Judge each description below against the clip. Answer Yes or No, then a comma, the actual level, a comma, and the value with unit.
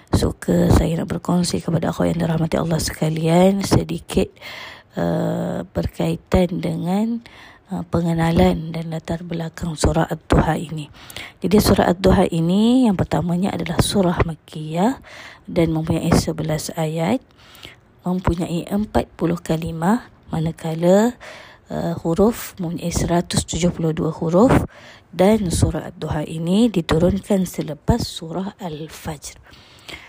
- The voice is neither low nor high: Yes, medium, 170 Hz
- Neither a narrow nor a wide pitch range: No, narrow, 2.3 semitones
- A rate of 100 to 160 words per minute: Yes, average, 105 wpm